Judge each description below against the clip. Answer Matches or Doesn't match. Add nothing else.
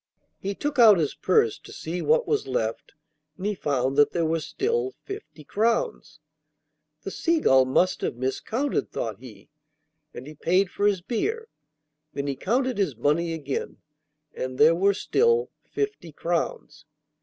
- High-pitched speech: Doesn't match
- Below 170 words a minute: Matches